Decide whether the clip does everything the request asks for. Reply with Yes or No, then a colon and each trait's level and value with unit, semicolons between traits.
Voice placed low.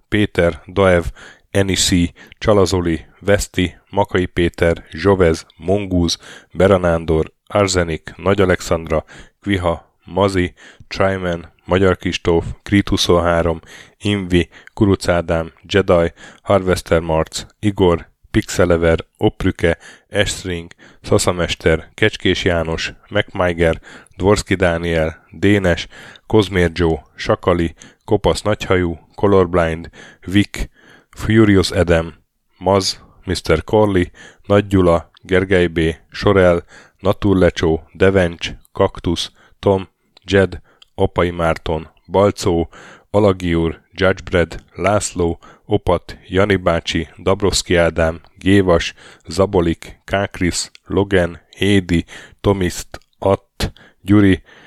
Yes: very low, 90 Hz